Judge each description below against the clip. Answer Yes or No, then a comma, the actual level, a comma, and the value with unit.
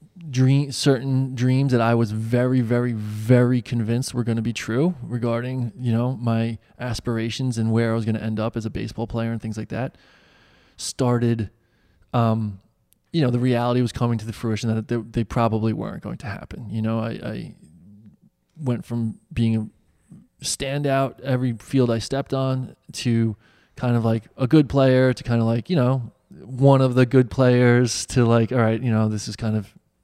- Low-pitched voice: Yes, low, 120 Hz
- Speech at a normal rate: Yes, average, 195 wpm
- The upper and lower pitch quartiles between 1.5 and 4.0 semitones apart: Yes, narrow, 2.4 semitones